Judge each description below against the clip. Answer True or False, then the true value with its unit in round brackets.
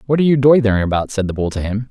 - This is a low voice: True (115 Hz)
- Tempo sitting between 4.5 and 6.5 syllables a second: False (8.0 syllables/s)